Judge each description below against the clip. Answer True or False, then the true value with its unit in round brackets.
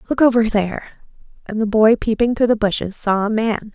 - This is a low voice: False (220 Hz)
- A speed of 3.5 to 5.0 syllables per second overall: False (5.7 syllables/s)